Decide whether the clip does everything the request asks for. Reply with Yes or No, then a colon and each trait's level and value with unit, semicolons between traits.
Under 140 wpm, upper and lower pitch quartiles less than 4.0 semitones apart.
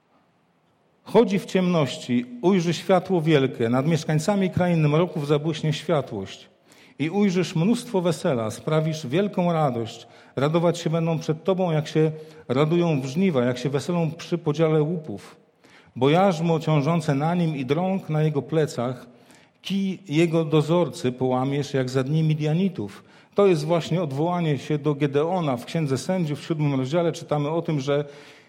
No: average, 145 wpm; average, 3.2 semitones